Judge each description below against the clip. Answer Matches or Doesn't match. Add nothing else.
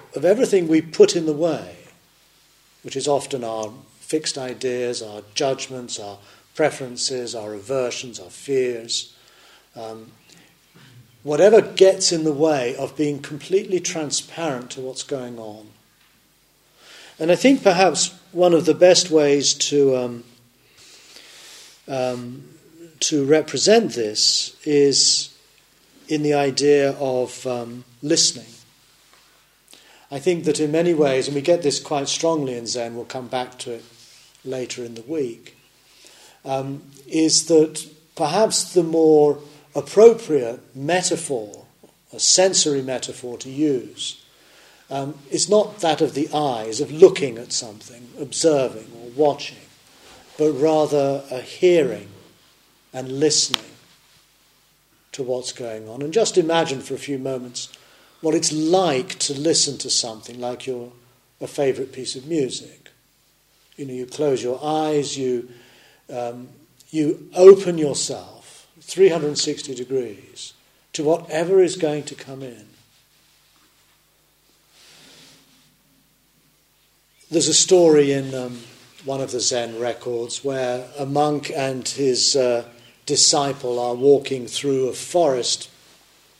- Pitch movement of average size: Matches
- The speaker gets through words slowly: Matches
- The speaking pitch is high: Doesn't match